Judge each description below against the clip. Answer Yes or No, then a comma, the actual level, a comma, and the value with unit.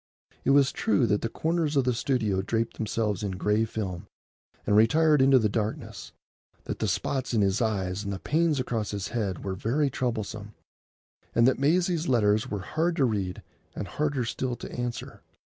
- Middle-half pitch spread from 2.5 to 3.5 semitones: No, average, 4.9 semitones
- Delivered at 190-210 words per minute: No, average, 180 wpm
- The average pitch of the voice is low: Yes, low, 115 Hz